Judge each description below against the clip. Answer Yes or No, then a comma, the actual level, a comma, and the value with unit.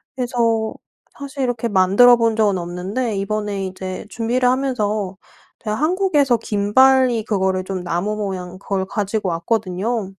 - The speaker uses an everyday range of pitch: Yes, average, 4.3 semitones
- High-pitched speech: Yes, high, 215 Hz